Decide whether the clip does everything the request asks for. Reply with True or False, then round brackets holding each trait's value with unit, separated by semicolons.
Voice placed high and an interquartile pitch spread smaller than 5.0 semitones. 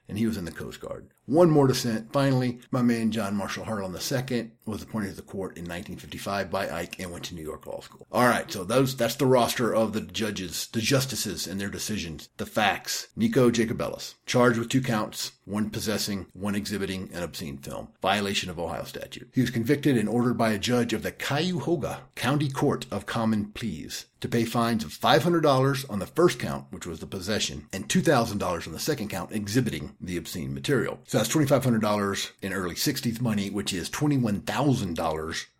False (115 Hz; 4.2 semitones)